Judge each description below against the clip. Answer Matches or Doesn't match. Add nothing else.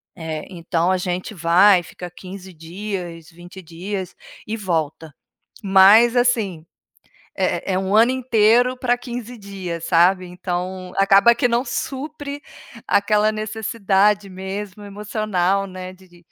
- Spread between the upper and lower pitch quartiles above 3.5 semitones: Doesn't match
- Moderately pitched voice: Doesn't match